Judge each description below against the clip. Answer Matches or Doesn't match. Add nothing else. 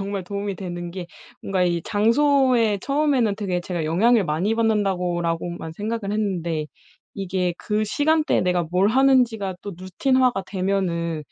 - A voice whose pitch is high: Matches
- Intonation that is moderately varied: Matches